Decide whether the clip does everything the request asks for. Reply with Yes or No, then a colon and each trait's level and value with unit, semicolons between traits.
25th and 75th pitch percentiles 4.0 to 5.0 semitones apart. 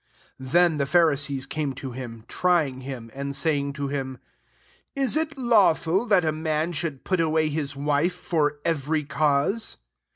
No: average, 3.5 semitones